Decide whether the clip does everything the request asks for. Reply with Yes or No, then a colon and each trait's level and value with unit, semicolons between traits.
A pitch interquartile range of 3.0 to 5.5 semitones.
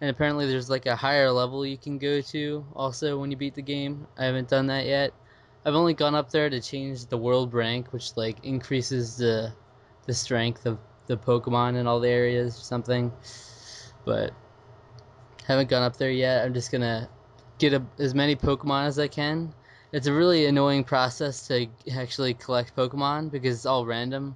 No: narrow, 2.4 semitones